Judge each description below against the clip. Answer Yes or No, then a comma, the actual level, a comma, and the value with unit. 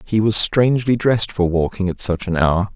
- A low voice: Yes, low, 100 Hz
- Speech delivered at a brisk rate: Yes, fast, 220 wpm